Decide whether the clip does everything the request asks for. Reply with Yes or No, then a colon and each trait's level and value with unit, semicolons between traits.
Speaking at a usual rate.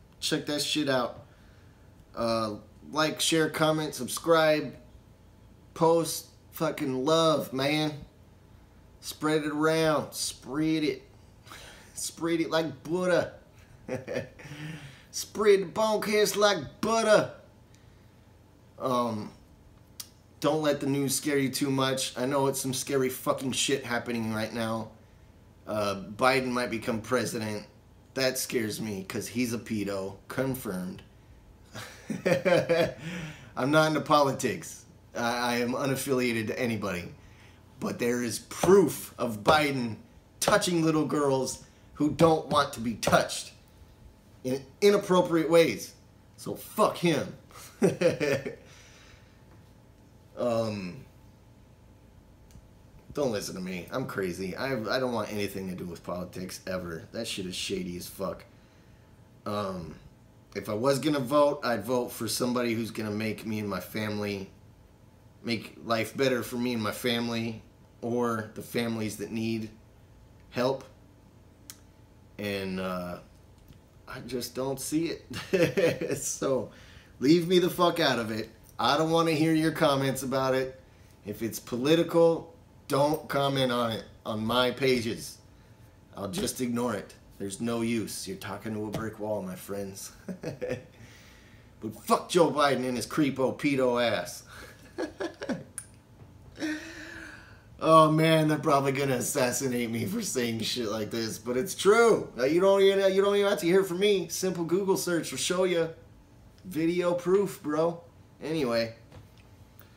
No: slow, 130 wpm